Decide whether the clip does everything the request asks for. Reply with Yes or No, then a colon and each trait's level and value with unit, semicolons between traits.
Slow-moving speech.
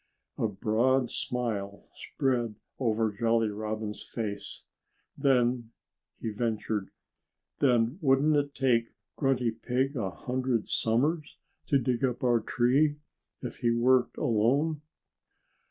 Yes: slow, 115 wpm